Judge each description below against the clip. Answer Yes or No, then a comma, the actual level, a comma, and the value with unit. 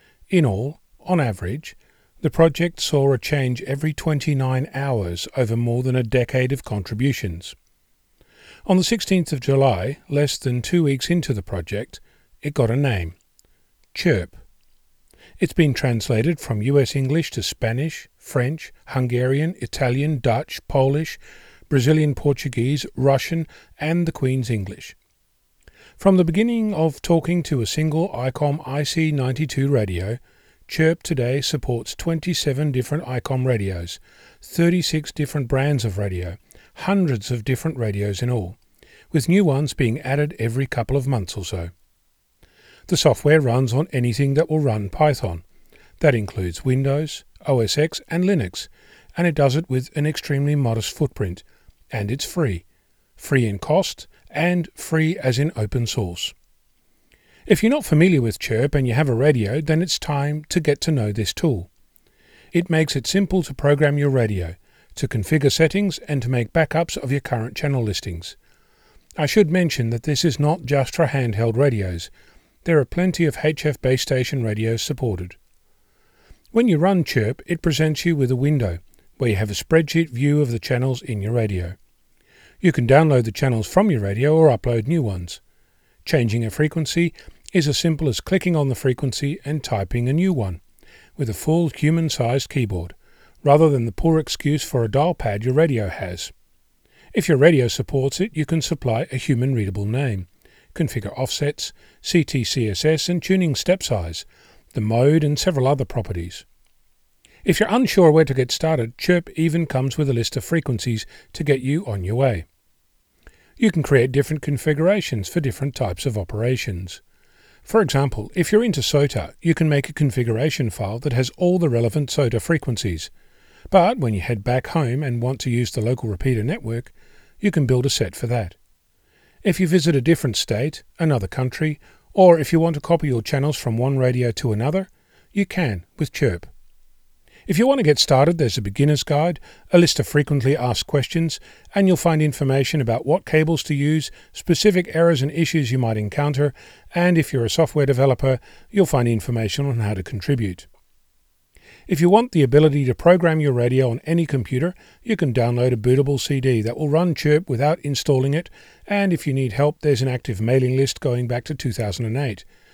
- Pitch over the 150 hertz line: No, medium, 140 Hz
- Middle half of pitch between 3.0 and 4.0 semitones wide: No, average, 5.1 semitones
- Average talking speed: Yes, average, 170 wpm